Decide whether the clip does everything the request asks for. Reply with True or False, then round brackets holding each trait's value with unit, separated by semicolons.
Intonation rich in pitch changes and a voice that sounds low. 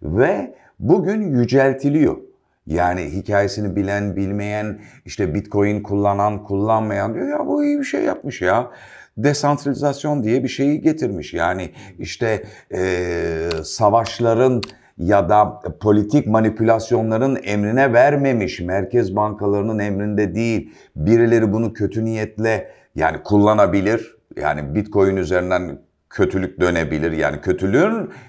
False (3.6 semitones; 105 Hz)